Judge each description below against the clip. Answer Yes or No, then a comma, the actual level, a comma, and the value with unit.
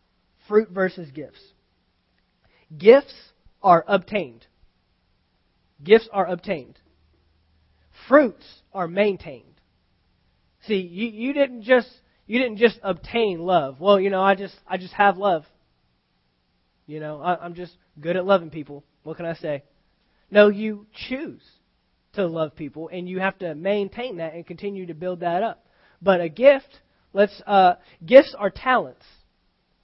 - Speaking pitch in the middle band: Yes, medium, 180 Hz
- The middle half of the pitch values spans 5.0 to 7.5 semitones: Yes, wide, 5.5 semitones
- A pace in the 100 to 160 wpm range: Yes, average, 140 wpm